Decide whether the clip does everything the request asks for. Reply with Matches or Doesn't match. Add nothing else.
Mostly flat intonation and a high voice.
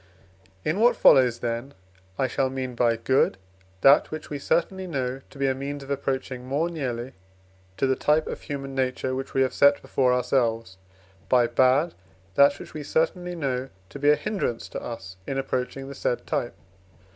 Doesn't match